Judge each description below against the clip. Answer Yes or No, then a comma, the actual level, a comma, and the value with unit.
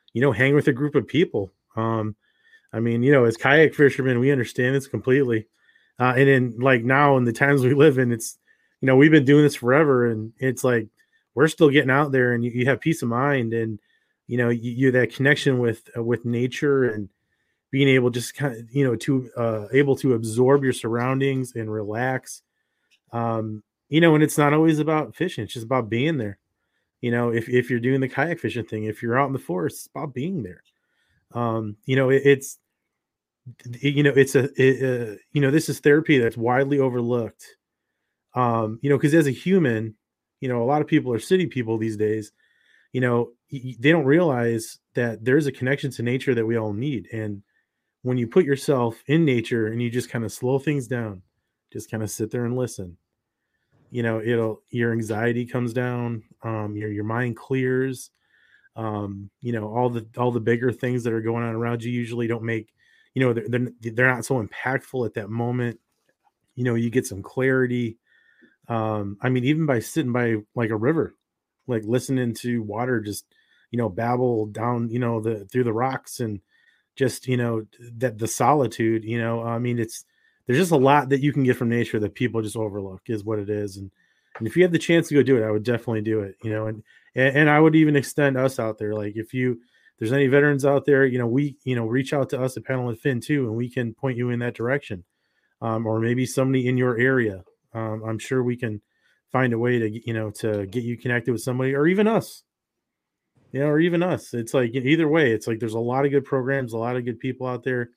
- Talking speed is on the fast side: Yes, fast, 225 wpm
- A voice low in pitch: Yes, low, 125 Hz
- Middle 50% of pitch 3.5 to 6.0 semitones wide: No, average, 3.1 semitones